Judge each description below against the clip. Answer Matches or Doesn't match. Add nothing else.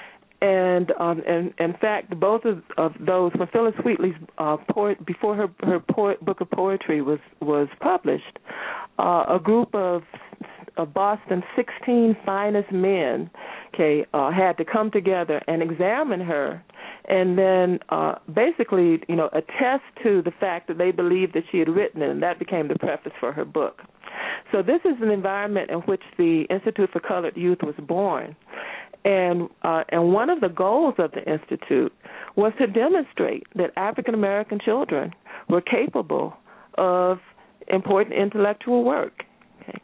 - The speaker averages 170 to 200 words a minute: Doesn't match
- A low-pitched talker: Doesn't match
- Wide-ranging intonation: Doesn't match